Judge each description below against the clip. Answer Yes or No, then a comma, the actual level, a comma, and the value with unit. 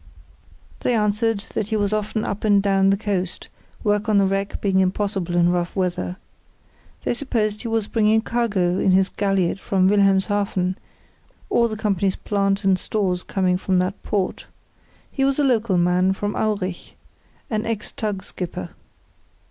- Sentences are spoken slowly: No, average, 160 wpm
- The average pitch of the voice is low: No, high, 200 Hz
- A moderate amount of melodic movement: No, narrow, 2.3 semitones